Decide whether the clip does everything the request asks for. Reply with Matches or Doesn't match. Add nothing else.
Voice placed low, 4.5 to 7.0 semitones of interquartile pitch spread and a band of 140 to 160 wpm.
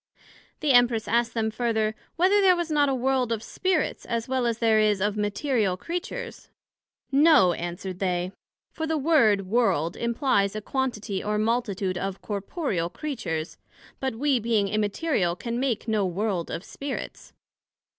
Doesn't match